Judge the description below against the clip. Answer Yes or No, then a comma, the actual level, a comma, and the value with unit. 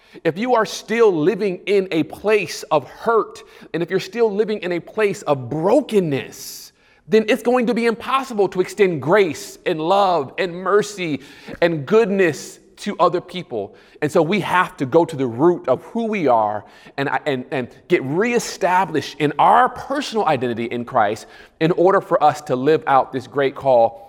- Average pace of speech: Yes, average, 180 wpm